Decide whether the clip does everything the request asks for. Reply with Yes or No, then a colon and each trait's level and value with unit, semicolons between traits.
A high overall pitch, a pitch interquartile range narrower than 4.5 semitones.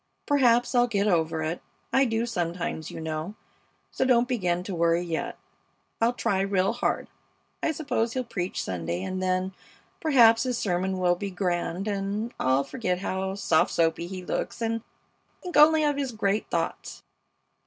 No: high, 195 Hz; average, 5.1 semitones